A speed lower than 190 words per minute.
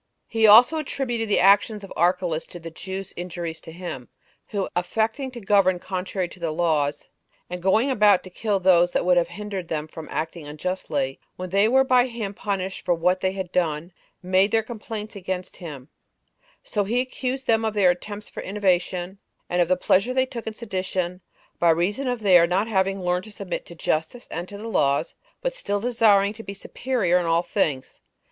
No: average, 195 wpm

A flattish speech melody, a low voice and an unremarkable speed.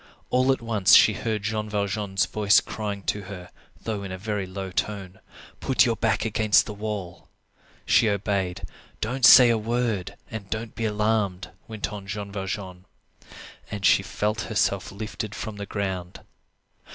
Yes: narrow, 2.1 semitones; low, 105 Hz; average, 160 wpm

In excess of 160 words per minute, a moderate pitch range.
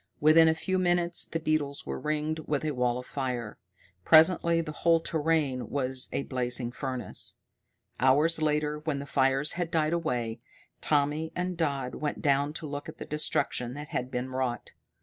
Yes: average, 170 wpm; average, 3.5 semitones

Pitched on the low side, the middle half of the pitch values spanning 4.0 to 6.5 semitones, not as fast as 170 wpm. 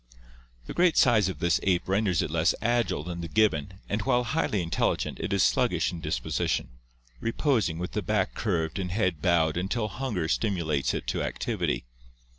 No: very low, 95 Hz; average, 4.5 semitones; average, 175 wpm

